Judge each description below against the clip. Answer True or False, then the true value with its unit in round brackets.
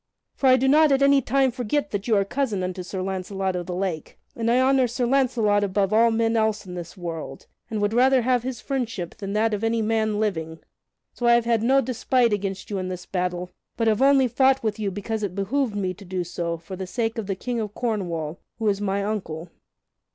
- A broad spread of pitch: False (4.4 semitones)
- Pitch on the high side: True (215 Hz)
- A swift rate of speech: True (230 wpm)